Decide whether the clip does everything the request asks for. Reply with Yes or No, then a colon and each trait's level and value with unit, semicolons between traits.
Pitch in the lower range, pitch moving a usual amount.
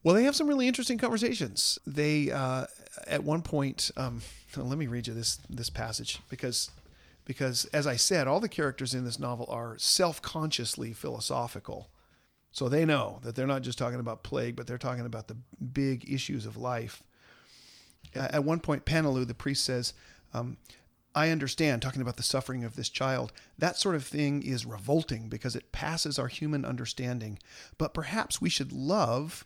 Yes: low, 130 Hz; average, 3.8 semitones